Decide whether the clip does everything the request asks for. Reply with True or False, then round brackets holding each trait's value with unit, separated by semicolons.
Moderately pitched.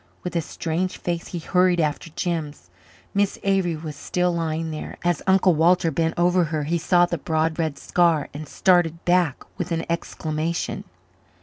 True (170 Hz)